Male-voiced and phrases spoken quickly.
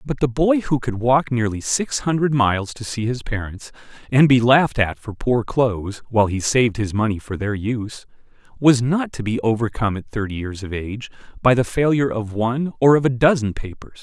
Yes: male; fast, 210 wpm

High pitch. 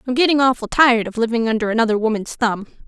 Yes: high, 235 Hz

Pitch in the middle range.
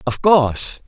Yes: medium, 145 Hz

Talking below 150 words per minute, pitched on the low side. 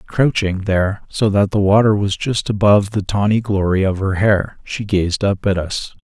No: average, 200 wpm; low, 100 Hz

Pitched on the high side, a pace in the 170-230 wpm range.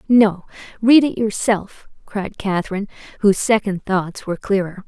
No: high, 205 Hz; slow, 135 wpm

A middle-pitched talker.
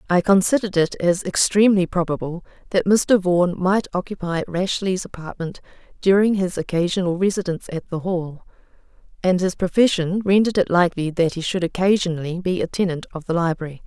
Yes: medium, 180 Hz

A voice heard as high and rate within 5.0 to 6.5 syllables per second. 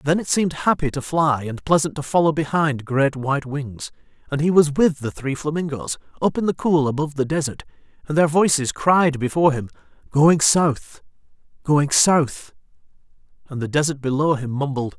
No: medium, 145 Hz; 5.3 syllables/s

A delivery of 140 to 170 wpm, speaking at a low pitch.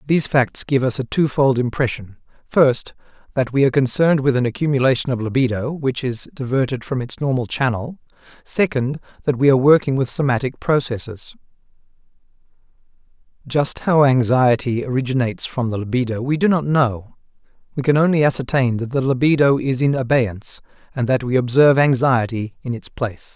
Yes: average, 155 wpm; low, 130 Hz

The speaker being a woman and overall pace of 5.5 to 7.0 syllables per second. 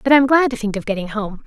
Yes: female; 6.3 syllables/s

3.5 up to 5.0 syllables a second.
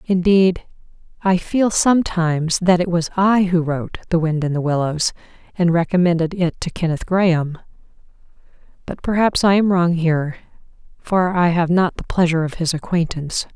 No: 5.3 syllables/s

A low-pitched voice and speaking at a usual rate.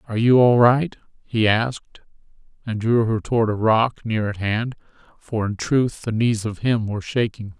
Yes: low, 115 Hz; average, 180 wpm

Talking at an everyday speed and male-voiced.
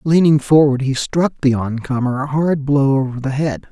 Yes: average, 195 wpm; male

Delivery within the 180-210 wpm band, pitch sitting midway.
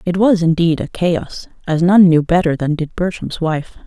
Yes: average, 200 wpm; medium, 170 Hz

